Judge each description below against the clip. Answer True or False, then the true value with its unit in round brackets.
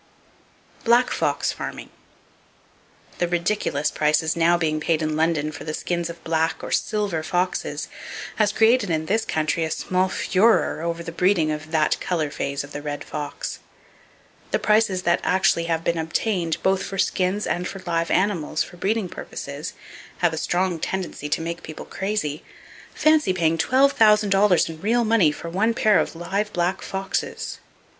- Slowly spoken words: False (165 wpm)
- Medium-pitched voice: True (175 Hz)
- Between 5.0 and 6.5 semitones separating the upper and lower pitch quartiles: False (3.8 semitones)